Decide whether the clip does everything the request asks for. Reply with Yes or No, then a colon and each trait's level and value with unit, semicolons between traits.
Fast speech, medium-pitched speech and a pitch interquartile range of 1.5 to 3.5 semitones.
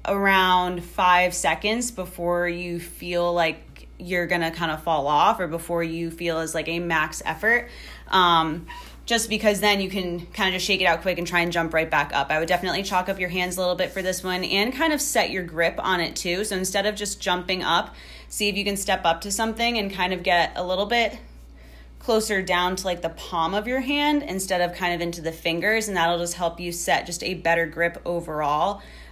Yes: fast, 230 wpm; medium, 180 Hz; narrow, 2.4 semitones